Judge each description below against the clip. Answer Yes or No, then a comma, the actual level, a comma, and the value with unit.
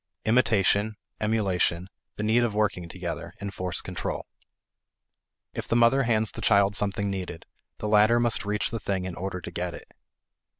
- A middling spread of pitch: Yes, average, 3.0 semitones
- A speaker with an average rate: Yes, average, 160 wpm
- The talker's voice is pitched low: Yes, low, 100 Hz